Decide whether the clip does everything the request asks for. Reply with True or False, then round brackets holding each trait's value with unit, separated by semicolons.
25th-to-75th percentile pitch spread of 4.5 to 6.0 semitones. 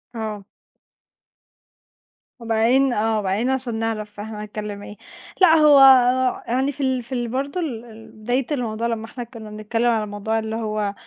False (2.7 semitones)